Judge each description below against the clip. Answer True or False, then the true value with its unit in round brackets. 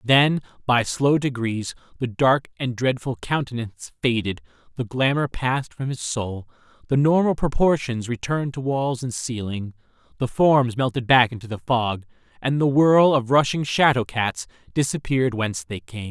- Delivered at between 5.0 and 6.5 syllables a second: False (4.7 syllables/s)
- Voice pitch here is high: False (125 Hz)